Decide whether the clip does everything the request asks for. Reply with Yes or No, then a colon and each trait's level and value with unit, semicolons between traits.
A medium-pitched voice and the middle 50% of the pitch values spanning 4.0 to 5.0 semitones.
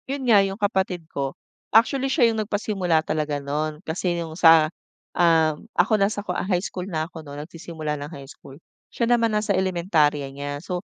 Yes: medium, 175 Hz; average, 4.7 semitones